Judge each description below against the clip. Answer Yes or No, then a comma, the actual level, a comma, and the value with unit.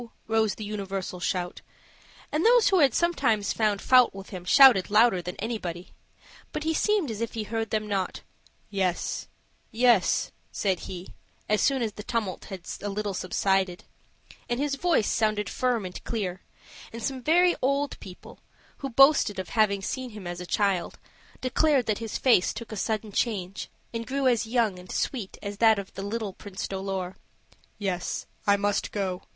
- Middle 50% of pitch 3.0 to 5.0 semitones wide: Yes, average, 4.1 semitones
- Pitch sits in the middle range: No, high, 215 Hz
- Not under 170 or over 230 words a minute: Yes, average, 175 wpm